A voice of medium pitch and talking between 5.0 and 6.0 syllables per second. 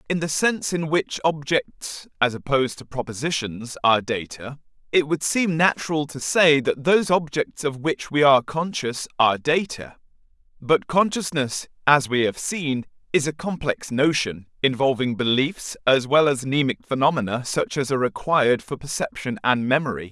No: medium, 145 Hz; 4.6 syllables/s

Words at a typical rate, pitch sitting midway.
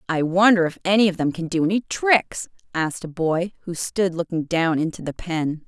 No: fast, 210 wpm; medium, 175 Hz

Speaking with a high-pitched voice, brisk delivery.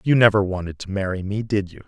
No: low, 100 Hz; fast, 255 wpm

